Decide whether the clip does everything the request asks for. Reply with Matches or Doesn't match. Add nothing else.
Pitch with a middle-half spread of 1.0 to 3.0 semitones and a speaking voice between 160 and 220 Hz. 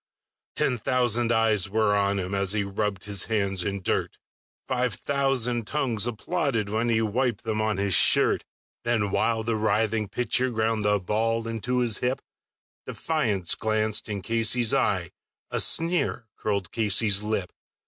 Doesn't match